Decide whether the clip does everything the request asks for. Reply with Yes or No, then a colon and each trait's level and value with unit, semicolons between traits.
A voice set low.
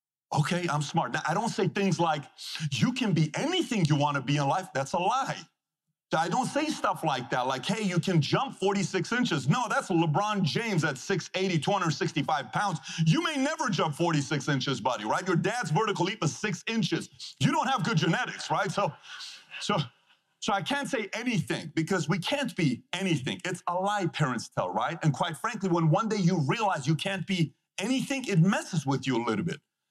No: medium, 175 Hz